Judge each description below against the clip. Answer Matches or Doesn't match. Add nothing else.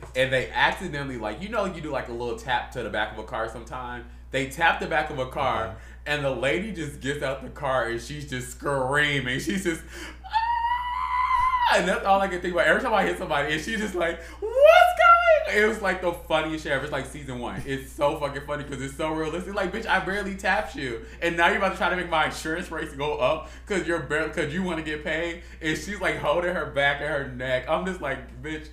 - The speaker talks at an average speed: Doesn't match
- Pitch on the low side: Doesn't match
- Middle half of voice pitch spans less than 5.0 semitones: Doesn't match